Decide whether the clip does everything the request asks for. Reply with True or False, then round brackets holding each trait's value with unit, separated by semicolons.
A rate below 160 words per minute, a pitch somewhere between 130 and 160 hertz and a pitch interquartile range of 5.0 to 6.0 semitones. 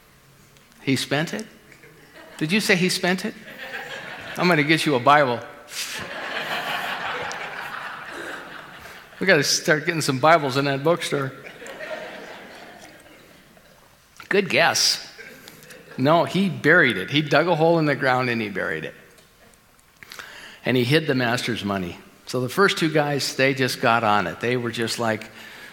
True (140 wpm; 140 Hz; 5.3 semitones)